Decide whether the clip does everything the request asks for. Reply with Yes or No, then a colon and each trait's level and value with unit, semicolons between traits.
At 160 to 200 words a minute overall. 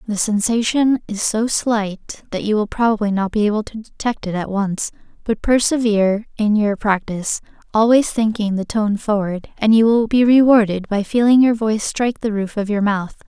Yes: average, 190 wpm